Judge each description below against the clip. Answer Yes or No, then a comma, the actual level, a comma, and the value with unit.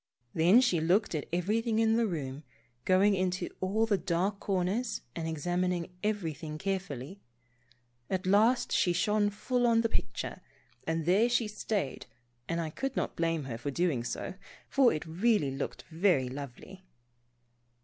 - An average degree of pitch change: Yes, average, 4.7 semitones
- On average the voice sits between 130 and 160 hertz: No, medium, 185 Hz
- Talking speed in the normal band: Yes, average, 150 wpm